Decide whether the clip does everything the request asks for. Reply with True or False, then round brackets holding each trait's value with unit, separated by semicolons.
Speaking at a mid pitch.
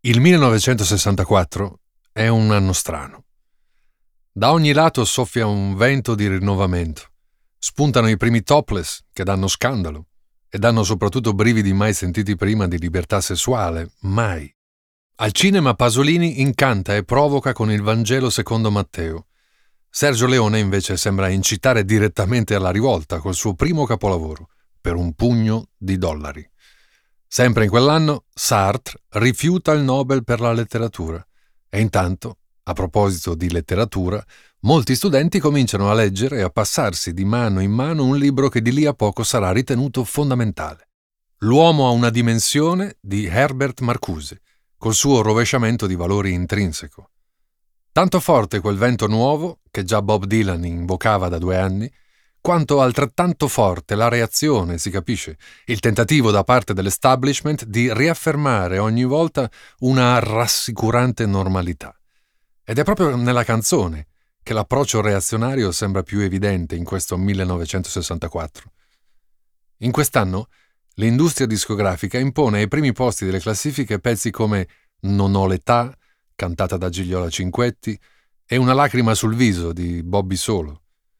False (110 Hz)